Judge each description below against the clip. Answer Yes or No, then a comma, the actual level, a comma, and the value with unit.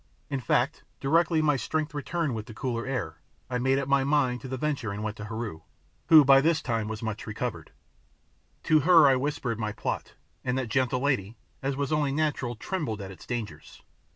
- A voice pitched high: No, low, 130 Hz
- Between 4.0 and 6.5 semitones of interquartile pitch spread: Yes, average, 4.5 semitones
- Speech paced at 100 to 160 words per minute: No, average, 200 wpm